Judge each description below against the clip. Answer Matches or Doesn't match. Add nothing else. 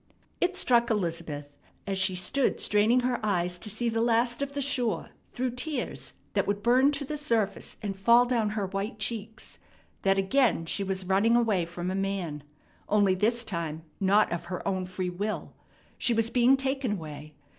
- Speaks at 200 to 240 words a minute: Doesn't match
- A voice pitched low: Doesn't match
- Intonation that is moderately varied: Matches